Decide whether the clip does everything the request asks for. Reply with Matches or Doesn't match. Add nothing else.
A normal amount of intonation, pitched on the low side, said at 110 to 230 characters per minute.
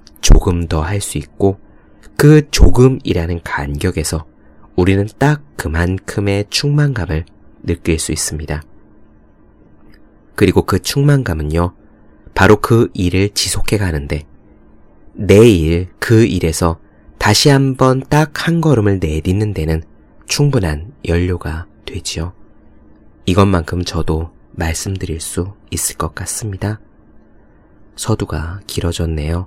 Matches